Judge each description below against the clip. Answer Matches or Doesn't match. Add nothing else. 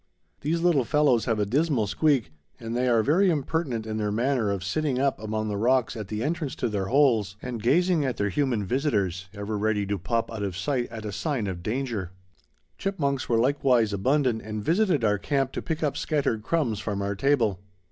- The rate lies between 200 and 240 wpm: Matches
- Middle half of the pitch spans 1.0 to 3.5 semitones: Doesn't match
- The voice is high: Doesn't match